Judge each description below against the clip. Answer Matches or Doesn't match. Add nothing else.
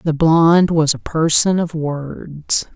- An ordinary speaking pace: Matches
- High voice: Doesn't match